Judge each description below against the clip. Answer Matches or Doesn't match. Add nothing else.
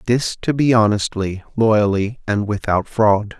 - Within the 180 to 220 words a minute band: Doesn't match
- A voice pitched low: Matches